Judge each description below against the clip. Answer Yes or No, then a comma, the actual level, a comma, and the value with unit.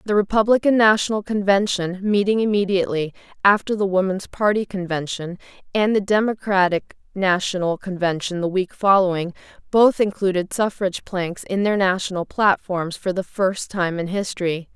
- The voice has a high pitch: Yes, high, 195 Hz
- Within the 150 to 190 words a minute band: No, slow, 135 wpm